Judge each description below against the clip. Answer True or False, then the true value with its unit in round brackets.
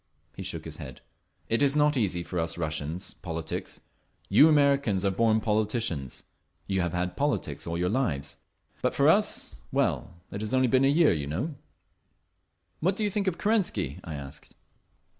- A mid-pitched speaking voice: False (105 Hz)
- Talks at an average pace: True (170 wpm)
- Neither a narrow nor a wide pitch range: False (8.8 semitones)